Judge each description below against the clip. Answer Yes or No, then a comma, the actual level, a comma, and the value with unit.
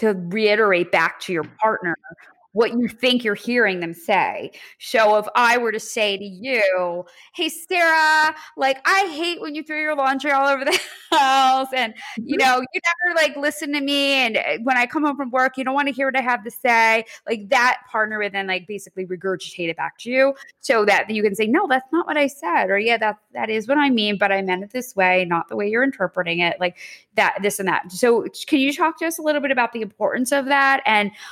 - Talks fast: Yes, fast, 240 wpm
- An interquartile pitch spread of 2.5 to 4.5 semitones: No, wide, 5.5 semitones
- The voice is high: Yes, high, 245 Hz